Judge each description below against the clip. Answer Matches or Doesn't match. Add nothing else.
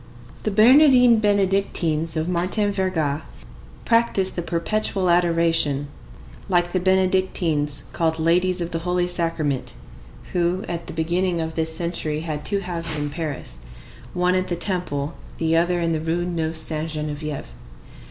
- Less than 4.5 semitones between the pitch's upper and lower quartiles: Matches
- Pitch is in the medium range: Matches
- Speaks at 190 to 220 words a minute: Doesn't match